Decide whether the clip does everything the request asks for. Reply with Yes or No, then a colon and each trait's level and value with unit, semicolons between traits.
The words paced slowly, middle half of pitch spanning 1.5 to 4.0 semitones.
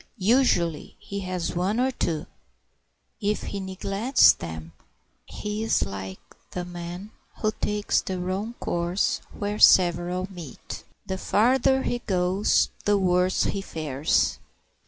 Yes: slow, 125 wpm; average, 3.2 semitones